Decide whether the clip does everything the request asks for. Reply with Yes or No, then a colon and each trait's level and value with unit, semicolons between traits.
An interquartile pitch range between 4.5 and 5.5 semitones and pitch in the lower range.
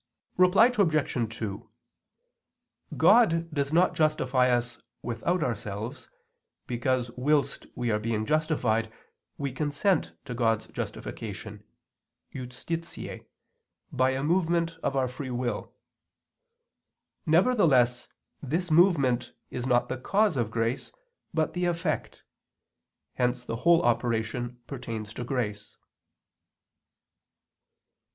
Yes: average, 5.2 semitones; low, 130 Hz